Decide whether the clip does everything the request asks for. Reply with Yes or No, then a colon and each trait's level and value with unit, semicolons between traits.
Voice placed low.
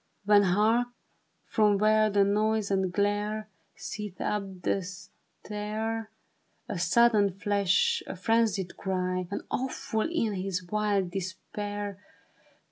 No: high, 205 Hz